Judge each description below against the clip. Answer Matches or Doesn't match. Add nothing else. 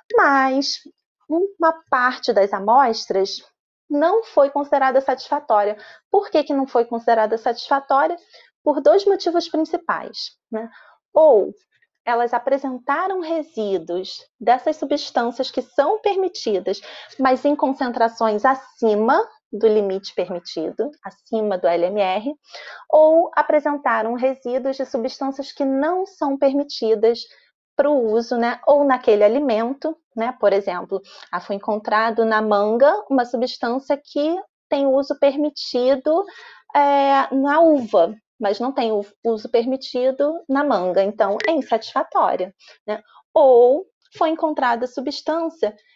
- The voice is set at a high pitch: Matches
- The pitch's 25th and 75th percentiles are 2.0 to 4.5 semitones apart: Doesn't match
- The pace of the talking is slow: Matches